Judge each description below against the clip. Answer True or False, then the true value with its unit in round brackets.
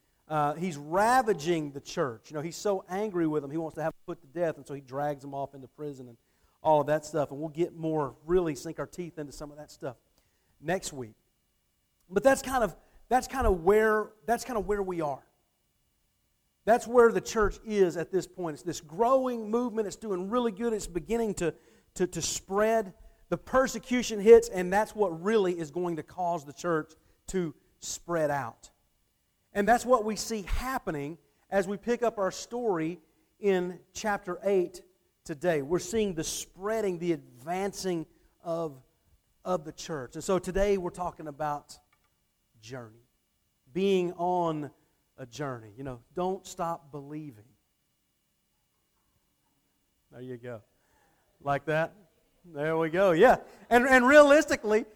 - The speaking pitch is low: False (175 Hz)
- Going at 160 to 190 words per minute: True (170 wpm)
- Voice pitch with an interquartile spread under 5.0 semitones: False (5.4 semitones)